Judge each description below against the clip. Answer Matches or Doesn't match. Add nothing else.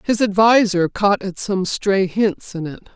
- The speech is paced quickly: Doesn't match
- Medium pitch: Doesn't match